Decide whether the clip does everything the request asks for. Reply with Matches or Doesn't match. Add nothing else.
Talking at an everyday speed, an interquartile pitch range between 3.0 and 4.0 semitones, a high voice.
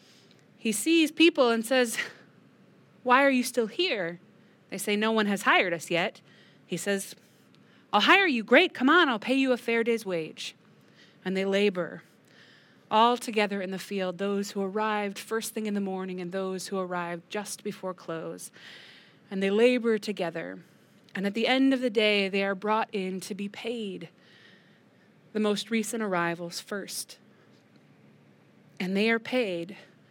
Matches